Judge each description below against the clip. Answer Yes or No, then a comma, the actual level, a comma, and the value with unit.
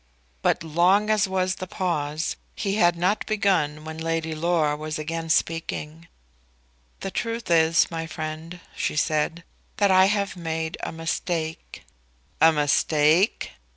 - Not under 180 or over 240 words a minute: No, slow, 135 wpm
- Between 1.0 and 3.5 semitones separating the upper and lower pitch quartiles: Yes, average, 2.9 semitones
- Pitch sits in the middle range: Yes, medium, 165 Hz